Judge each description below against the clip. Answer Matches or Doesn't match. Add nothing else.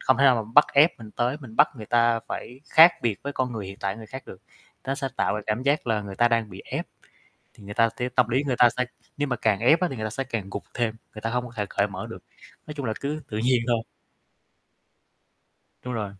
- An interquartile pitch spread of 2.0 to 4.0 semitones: Matches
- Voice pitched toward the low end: Matches